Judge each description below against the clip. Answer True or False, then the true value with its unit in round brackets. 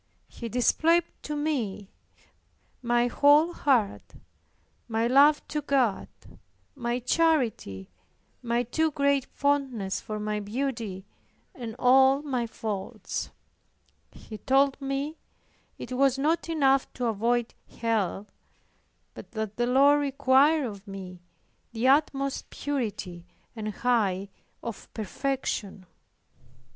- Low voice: False (250 Hz)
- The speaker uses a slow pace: True (110 wpm)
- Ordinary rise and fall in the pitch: True (4.6 semitones)